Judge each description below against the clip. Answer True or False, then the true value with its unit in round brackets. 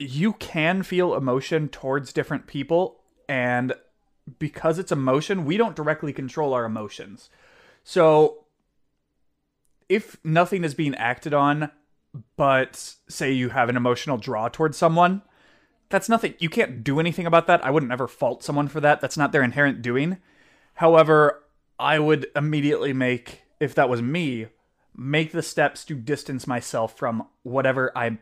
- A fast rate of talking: False (150 wpm)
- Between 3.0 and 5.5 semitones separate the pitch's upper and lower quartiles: True (3.9 semitones)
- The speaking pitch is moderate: True (150 Hz)